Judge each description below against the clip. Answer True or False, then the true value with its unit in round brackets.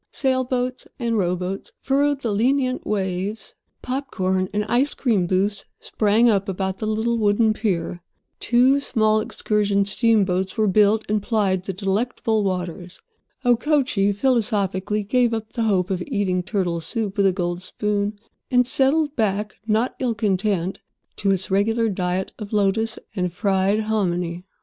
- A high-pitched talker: True (210 Hz)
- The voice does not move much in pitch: False (3.3 semitones)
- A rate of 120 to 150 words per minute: True (145 wpm)